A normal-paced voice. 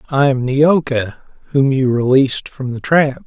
Yes: average, 165 wpm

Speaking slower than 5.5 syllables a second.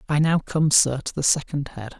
Yes: 5.1 syllables/s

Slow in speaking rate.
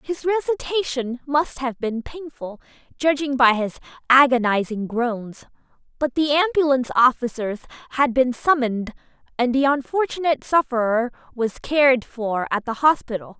Yes: slow, 125 wpm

